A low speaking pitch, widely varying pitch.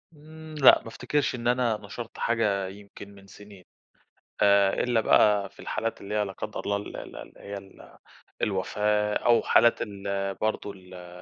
No: low, 105 Hz; average, 2.7 semitones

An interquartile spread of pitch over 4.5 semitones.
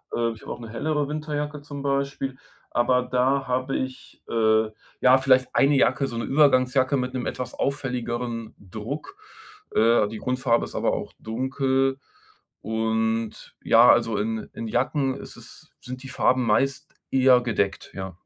No: average, 2.9 semitones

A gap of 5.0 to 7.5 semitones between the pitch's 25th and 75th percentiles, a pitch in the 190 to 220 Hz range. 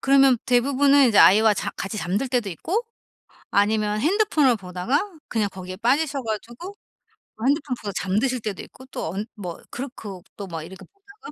No: wide, 5.6 semitones; high, 235 Hz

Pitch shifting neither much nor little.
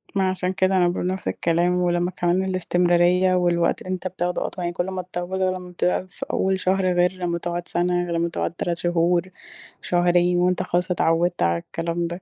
No: narrow, 1.1 semitones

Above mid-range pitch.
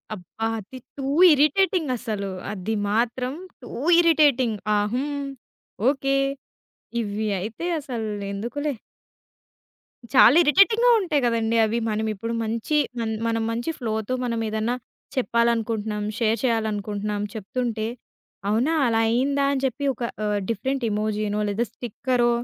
Yes: high, 230 Hz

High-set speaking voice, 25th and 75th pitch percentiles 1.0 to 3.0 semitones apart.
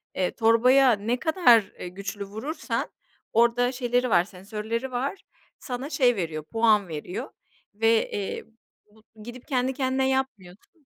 No: high, 230 Hz; average, 4.0 semitones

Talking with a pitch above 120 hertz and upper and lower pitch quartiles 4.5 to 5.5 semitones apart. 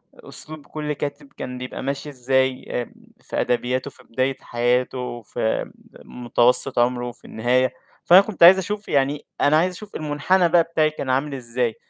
No: low, 135 Hz; average, 3.7 semitones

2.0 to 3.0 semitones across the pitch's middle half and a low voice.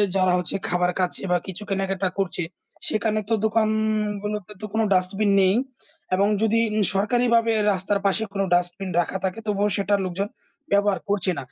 No: narrow, 2.4 semitones; high, 200 Hz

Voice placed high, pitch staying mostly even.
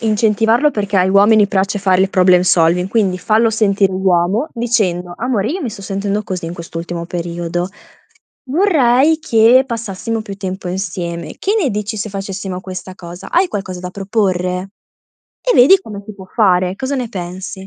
No: high, 195 Hz; average, 3.6 semitones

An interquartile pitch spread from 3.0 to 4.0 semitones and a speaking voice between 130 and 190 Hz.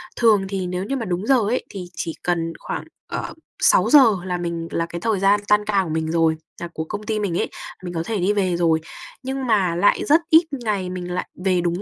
Yes: average, 3.7 semitones; medium, 185 Hz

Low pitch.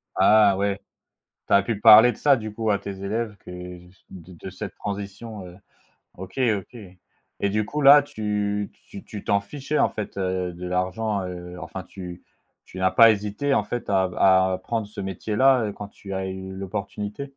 Yes: low, 100 Hz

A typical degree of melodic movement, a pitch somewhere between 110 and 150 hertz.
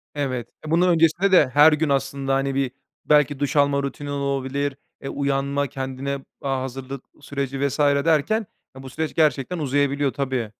No: narrow, 1.5 semitones; medium, 140 Hz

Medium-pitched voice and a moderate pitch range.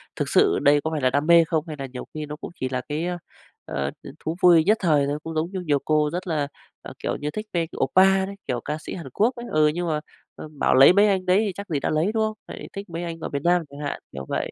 Yes: medium, 160 Hz; average, 3.8 semitones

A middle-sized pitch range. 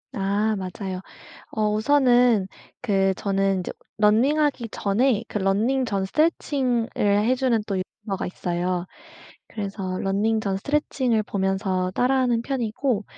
Yes: average, 4.3 semitones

